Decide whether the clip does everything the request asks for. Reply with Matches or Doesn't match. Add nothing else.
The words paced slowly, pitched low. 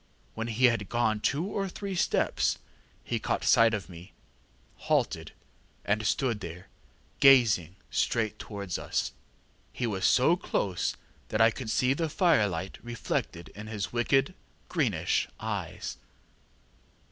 Matches